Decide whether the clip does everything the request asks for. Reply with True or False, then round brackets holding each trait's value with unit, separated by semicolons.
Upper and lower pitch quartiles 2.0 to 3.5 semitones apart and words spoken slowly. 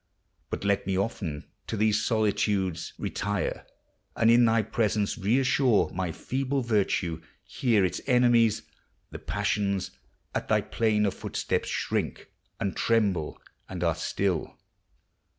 True (3.2 semitones; 120 wpm)